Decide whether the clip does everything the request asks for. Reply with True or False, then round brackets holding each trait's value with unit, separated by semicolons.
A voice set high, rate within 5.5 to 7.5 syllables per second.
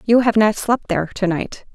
False (210 Hz; 5.3 syllables/s)